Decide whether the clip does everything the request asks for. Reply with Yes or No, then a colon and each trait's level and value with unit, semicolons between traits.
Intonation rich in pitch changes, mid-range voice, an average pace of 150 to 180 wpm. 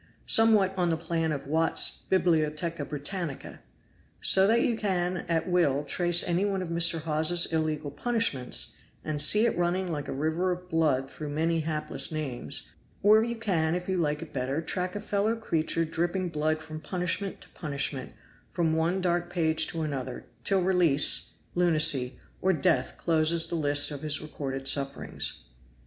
No: average, 3.0 semitones; medium, 165 Hz; average, 165 wpm